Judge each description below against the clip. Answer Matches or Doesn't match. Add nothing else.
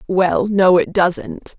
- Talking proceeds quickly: Doesn't match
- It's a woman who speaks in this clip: Matches